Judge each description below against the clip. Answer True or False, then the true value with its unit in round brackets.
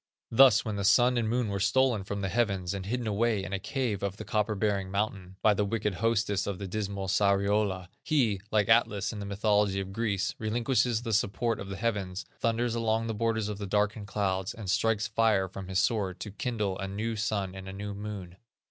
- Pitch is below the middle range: True (105 Hz)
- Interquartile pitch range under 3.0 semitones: True (2.5 semitones)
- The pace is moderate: False (215 wpm)